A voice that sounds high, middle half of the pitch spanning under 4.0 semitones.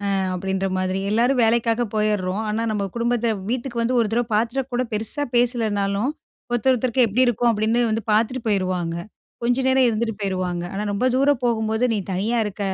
Yes: high, 225 Hz; average, 3.1 semitones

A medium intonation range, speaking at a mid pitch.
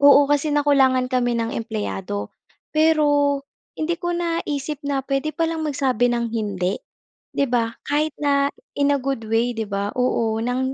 No: average, 3.9 semitones; very high, 275 Hz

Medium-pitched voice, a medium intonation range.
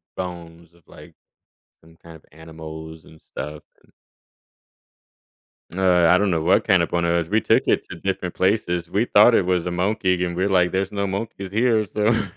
No: very low, 90 Hz; average, 3.0 semitones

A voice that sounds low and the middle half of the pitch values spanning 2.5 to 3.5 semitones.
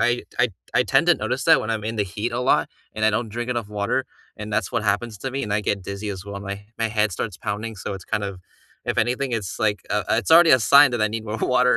Yes: low, 110 Hz; average, 2.8 semitones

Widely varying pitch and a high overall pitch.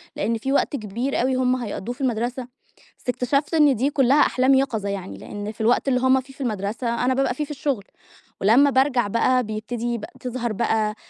No: average, 3.3 semitones; very high, 250 Hz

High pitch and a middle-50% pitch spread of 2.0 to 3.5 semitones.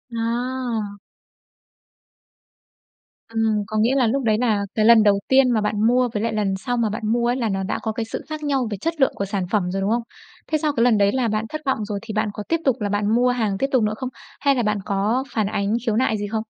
Yes: high, 225 Hz; average, 3.0 semitones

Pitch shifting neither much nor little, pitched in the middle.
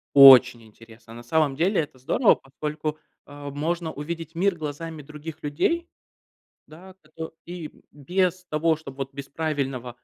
Yes: average, 3.3 semitones; medium, 150 Hz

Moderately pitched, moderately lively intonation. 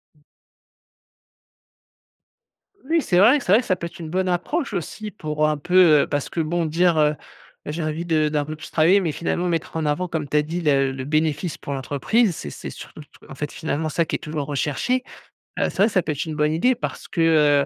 Yes: medium, 160 Hz; average, 3.1 semitones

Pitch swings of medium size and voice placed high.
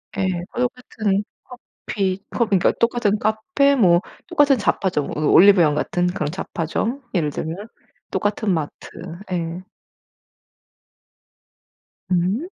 Yes: average, 4.8 semitones; high, 195 Hz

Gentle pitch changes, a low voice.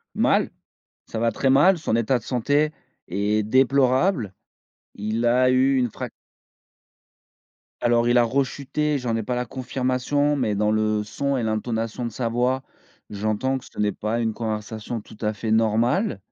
No: average, 3.3 semitones; low, 120 Hz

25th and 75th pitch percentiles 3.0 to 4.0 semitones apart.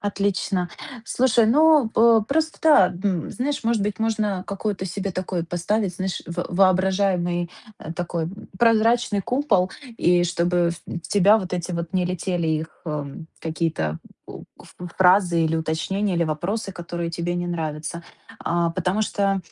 Yes: average, 3.3 semitones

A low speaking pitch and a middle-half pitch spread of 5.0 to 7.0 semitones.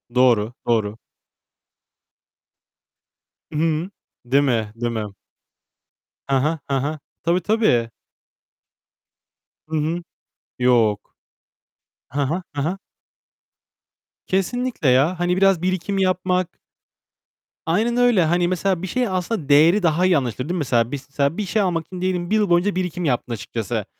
No: medium, 170 Hz; wide, 5.6 semitones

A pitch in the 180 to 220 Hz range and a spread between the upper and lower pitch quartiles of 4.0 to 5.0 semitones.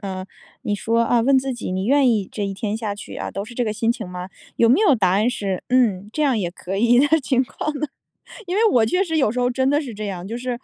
No: high, 230 Hz; average, 4.5 semitones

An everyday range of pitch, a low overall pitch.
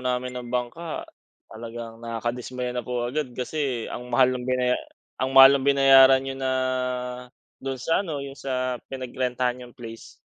No: narrow, 1.5 semitones; low, 125 Hz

